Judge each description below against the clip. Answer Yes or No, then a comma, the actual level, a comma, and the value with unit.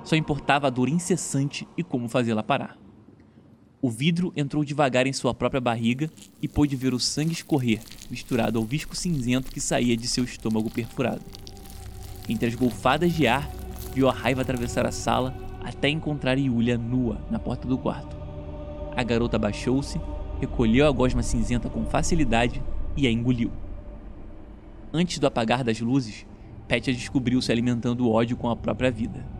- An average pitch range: Yes, average, 3.4 semitones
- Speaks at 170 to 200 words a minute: No, average, 160 wpm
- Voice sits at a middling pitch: No, low, 125 Hz